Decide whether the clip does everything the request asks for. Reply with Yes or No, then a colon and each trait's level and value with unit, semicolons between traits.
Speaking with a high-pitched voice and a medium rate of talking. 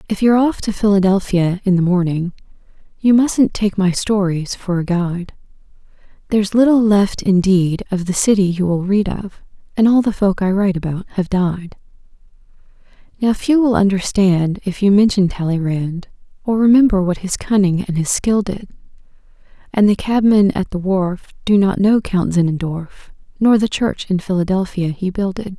Yes: high, 195 Hz; average, 165 wpm